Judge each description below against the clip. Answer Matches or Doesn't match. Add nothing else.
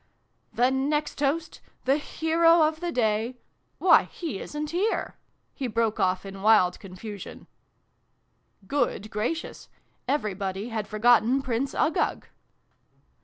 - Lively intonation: Matches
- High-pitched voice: Matches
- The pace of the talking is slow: Matches